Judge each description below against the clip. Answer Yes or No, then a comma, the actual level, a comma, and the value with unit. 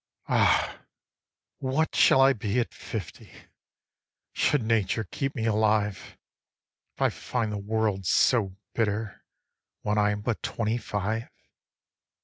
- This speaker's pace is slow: Yes, slow, 125 wpm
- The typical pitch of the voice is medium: No, low, 110 Hz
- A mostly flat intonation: Yes, narrow, 2.2 semitones